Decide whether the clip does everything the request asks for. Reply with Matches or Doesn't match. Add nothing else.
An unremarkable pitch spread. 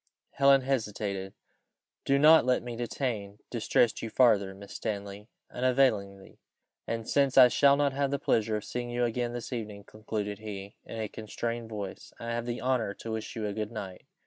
Matches